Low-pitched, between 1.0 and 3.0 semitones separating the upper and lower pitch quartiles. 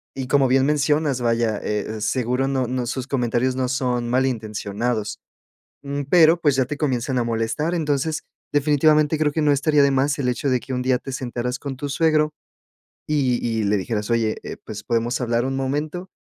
No: low, 130 Hz; average, 3.4 semitones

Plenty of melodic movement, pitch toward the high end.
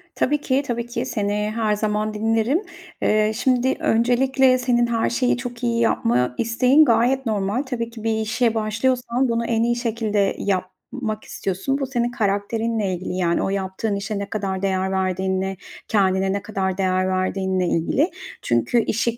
No: average, 3.8 semitones; high, 220 Hz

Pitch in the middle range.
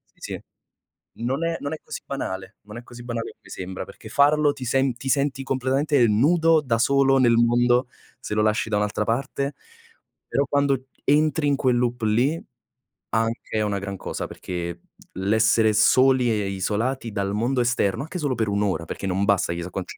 No: low, 120 Hz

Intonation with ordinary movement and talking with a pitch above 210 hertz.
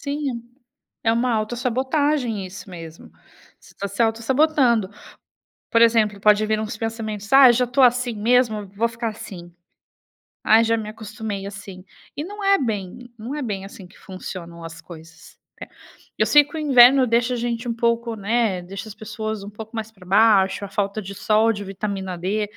Yes: average, 3.2 semitones; high, 220 Hz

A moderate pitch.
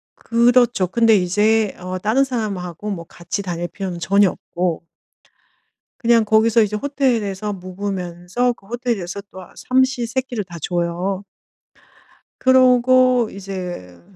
No: high, 205 Hz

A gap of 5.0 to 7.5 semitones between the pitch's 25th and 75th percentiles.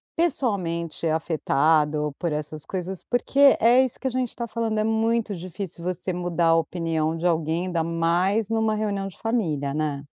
Yes: wide, 5.5 semitones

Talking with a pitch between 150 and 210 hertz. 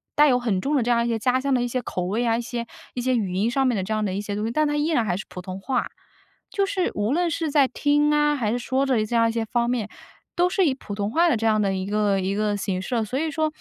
No: high, 235 Hz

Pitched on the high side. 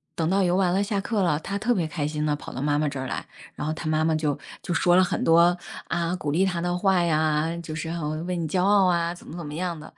No: medium, 170 Hz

